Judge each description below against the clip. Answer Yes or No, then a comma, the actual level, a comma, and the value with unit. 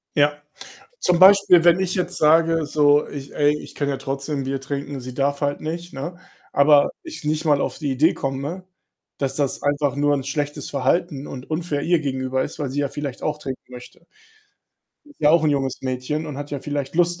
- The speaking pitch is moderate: Yes, medium, 145 Hz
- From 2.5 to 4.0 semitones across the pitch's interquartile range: Yes, average, 2.8 semitones